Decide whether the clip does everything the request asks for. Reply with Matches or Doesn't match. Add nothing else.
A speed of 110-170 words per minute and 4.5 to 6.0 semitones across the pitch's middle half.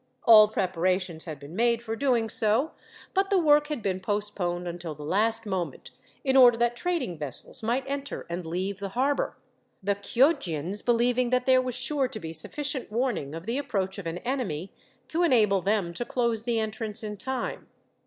Doesn't match